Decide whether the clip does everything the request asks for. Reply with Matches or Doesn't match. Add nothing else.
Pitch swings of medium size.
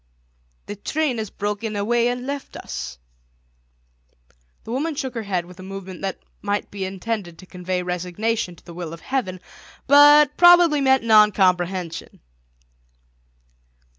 Doesn't match